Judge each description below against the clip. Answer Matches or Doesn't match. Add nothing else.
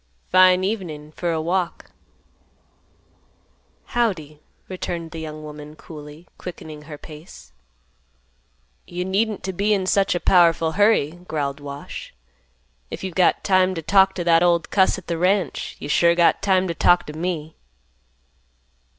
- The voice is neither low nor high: Matches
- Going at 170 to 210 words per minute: Doesn't match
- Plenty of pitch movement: Doesn't match